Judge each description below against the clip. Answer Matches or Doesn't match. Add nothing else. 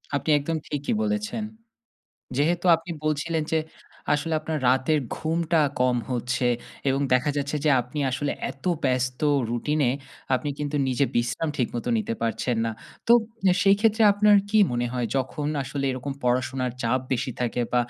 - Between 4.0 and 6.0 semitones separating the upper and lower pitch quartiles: Matches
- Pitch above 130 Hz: Matches